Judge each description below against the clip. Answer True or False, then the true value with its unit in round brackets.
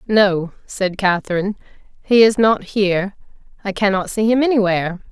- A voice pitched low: False (200 Hz)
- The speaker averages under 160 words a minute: True (140 wpm)